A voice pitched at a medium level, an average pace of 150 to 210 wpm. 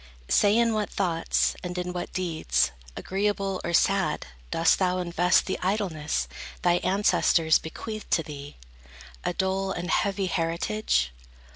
No: medium, 180 Hz; slow, 135 wpm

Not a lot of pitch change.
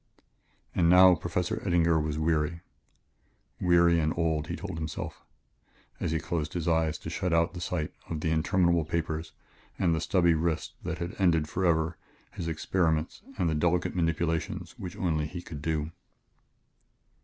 Yes: narrow, 1.7 semitones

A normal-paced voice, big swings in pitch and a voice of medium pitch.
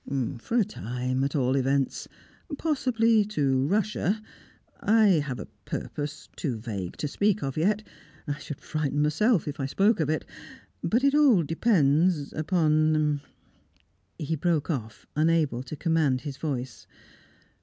Yes: average, 145 wpm; wide, 6.4 semitones; medium, 155 Hz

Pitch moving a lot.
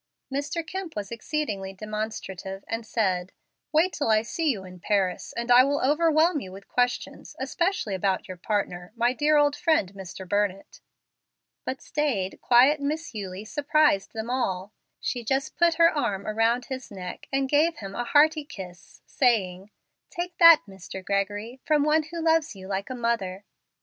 Yes: wide, 7.2 semitones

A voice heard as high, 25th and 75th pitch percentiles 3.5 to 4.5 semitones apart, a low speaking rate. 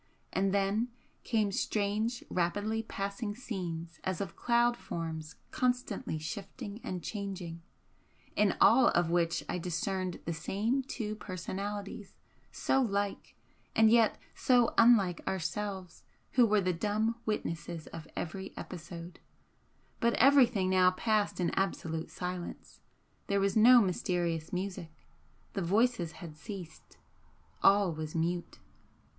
Yes: high, 195 Hz; average, 4.1 semitones; slow, 120 wpm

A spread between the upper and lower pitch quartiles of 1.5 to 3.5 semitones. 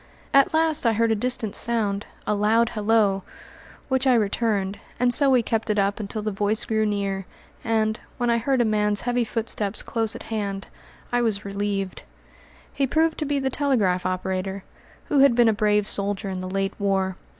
Yes: average, 3.1 semitones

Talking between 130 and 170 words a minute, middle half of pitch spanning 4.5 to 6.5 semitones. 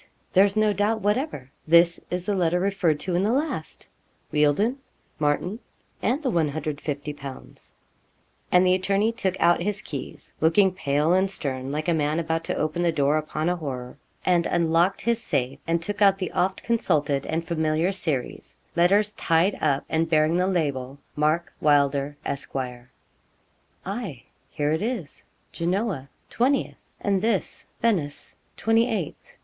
Yes: average, 150 wpm; average, 4.9 semitones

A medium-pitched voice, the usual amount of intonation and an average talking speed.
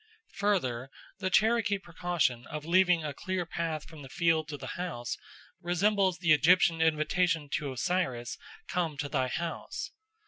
Yes: medium, 165 Hz; average, 3.8 semitones; average, 145 wpm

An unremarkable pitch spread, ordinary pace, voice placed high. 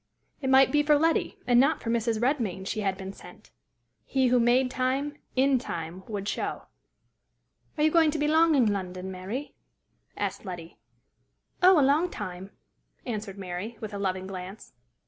No: wide, 6.4 semitones; average, 170 wpm; high, 230 Hz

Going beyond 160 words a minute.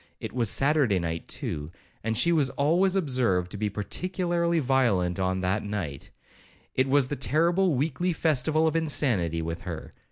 No: average, 155 wpm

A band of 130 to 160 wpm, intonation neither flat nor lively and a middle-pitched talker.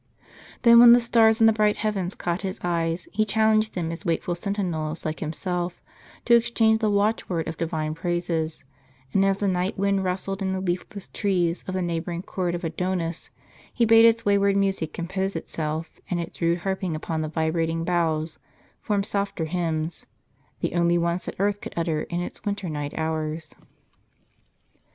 No: average, 175 wpm; average, 3.4 semitones; medium, 180 Hz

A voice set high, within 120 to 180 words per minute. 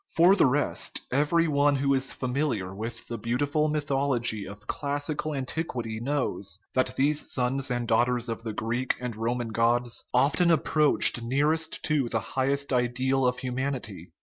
No: low, 130 Hz; average, 155 wpm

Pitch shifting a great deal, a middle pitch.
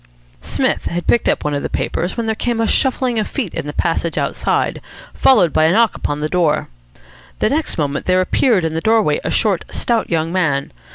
Yes: wide, 6.2 semitones; medium, 180 Hz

